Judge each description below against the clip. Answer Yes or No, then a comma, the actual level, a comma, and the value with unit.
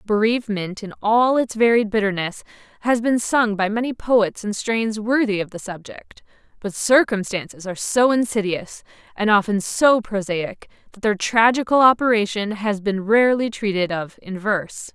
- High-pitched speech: Yes, high, 215 Hz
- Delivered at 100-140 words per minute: No, average, 155 wpm